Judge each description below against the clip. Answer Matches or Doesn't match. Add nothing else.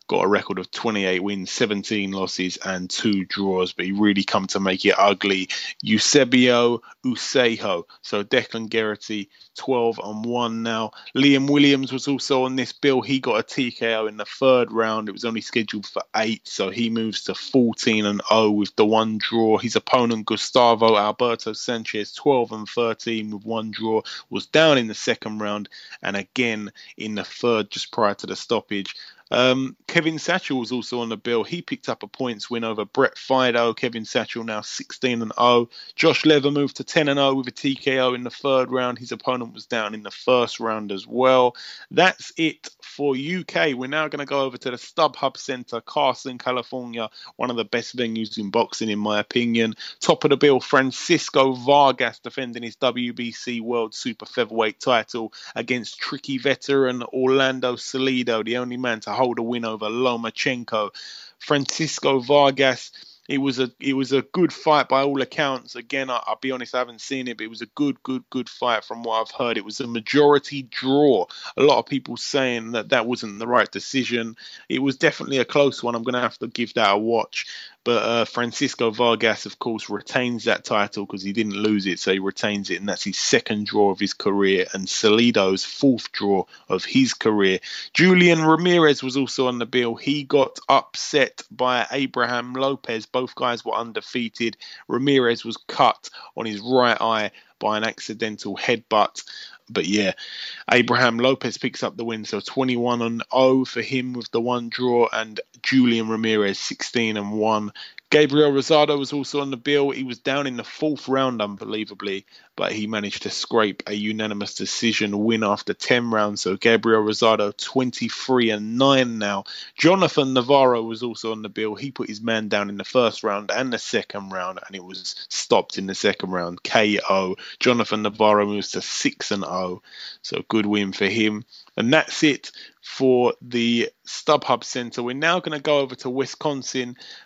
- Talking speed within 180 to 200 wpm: Matches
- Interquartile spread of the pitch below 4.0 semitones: Matches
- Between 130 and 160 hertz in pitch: Doesn't match